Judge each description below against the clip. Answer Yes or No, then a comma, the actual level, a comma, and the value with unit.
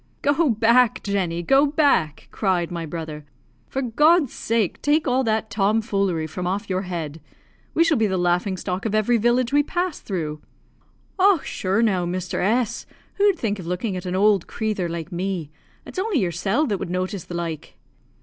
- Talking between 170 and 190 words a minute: Yes, average, 180 wpm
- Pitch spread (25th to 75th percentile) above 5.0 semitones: Yes, wide, 5.6 semitones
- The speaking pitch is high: Yes, high, 200 Hz